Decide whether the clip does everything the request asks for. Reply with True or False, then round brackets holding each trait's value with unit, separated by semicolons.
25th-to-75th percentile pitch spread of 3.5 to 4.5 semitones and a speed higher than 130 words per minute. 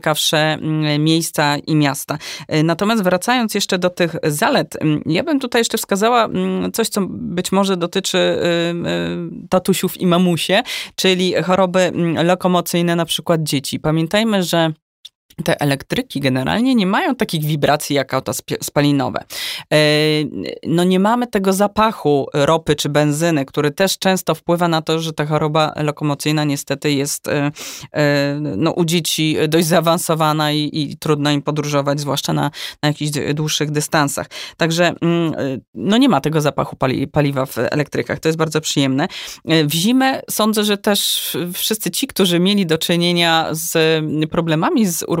True (3.8 semitones; 140 wpm)